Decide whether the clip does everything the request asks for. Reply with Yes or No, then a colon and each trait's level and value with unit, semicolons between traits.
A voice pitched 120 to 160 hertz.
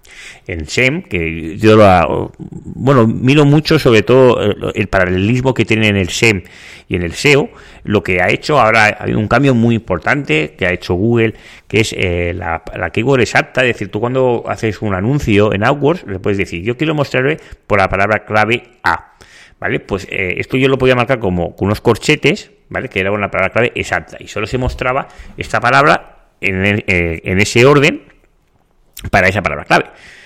No: low, 105 Hz